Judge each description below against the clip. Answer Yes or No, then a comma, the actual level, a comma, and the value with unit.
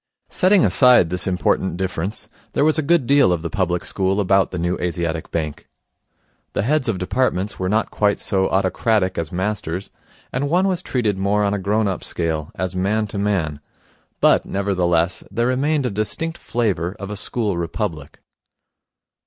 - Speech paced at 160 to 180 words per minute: Yes, average, 170 wpm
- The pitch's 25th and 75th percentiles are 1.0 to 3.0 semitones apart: No, average, 4.2 semitones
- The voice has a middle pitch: No, low, 100 Hz